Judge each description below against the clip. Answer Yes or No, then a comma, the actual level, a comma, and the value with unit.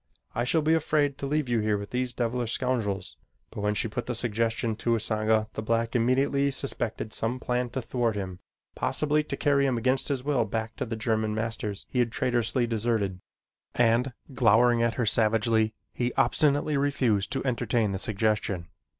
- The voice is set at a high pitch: No, low, 115 Hz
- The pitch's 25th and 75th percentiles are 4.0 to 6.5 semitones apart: No, average, 2.8 semitones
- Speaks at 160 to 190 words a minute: Yes, average, 180 wpm